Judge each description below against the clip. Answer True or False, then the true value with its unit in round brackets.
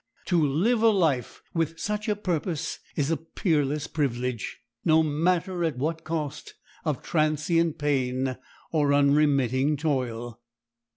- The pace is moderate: False (125 wpm)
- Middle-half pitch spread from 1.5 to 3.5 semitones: True (3.2 semitones)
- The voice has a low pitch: False (150 Hz)